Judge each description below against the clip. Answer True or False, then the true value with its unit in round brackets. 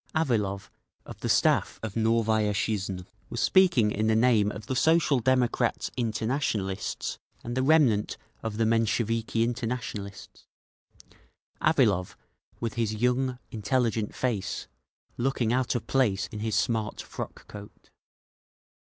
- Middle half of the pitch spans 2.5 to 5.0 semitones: True (2.8 semitones)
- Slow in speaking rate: True (125 wpm)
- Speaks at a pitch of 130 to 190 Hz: False (115 Hz)